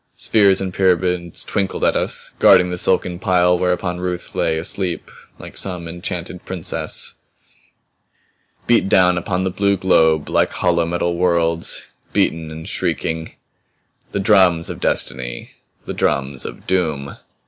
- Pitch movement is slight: Yes, narrow, 2.0 semitones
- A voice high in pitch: No, very low, 90 Hz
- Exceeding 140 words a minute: No, slow, 135 wpm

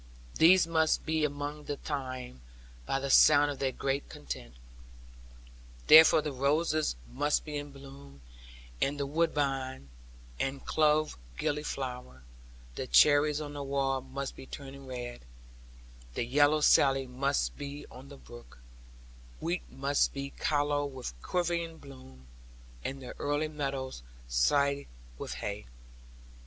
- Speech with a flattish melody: Yes, narrow, 2.0 semitones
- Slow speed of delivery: Yes, slow, 130 wpm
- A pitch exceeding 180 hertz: No, medium, 140 Hz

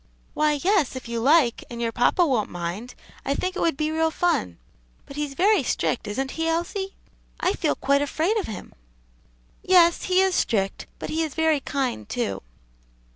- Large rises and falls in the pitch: Yes, wide, 5.9 semitones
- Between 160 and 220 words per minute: Yes, average, 180 wpm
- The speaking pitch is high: Yes, very high, 300 Hz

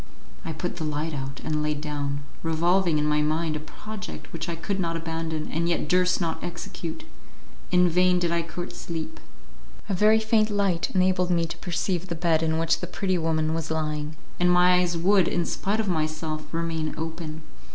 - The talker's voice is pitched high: No, medium, 165 Hz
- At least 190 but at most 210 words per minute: Yes, average, 195 wpm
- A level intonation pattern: Yes, narrow, 2.3 semitones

